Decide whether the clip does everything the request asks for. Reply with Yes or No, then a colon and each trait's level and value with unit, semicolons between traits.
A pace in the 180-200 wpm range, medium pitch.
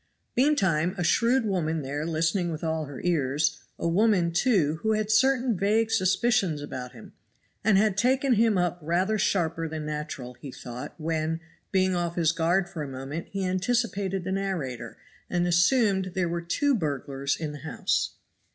No: average, 170 wpm; medium, 175 Hz